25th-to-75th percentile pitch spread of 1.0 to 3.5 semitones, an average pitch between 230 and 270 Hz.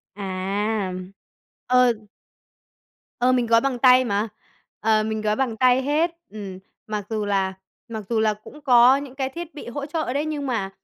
No: average, 3.9 semitones; high, 235 Hz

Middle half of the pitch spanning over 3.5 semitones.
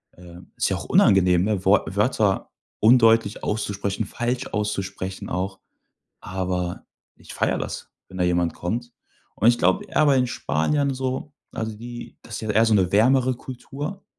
Yes: average, 4.5 semitones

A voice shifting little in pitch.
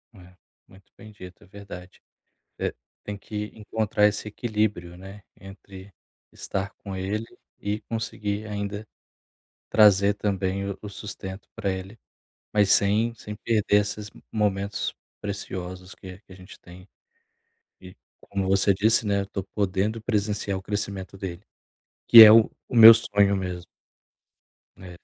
Yes: narrow, 1.8 semitones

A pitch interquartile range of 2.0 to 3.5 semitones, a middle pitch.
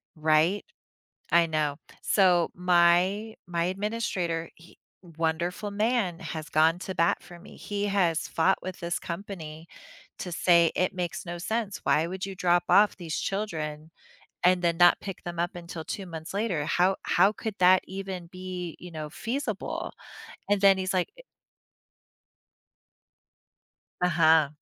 Yes: narrow, 2.6 semitones; medium, 180 Hz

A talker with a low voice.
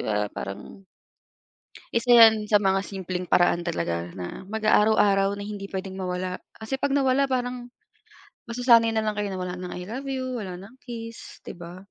No: high, 205 Hz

